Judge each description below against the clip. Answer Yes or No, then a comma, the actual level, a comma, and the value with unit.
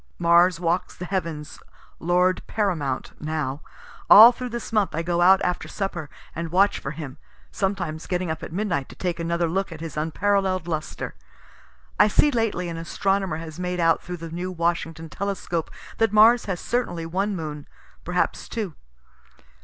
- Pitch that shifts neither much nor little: Yes, average, 3.0 semitones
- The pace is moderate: Yes, average, 165 wpm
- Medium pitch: Yes, medium, 175 Hz